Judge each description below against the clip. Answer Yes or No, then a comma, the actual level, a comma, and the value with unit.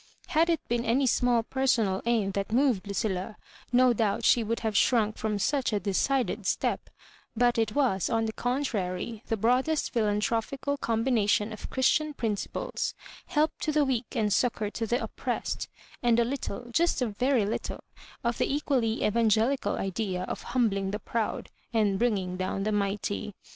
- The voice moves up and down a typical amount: Yes, average, 3.4 semitones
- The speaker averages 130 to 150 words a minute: No, average, 165 wpm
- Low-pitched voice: No, high, 230 Hz